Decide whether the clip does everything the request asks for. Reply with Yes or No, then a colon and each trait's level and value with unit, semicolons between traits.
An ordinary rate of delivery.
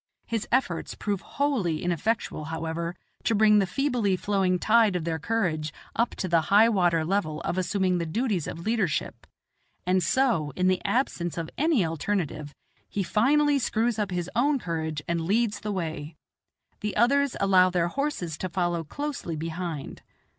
Yes: average, 160 wpm